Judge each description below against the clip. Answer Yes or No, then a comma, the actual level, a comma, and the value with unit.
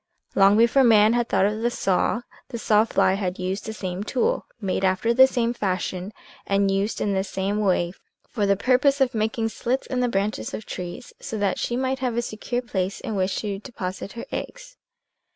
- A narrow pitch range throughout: No, average, 3.6 semitones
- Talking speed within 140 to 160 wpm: No, fast, 205 wpm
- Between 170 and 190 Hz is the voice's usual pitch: No, high, 215 Hz